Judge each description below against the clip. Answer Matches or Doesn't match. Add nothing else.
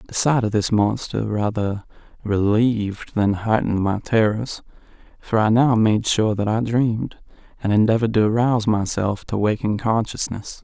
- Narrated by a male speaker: Matches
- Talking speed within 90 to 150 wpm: Matches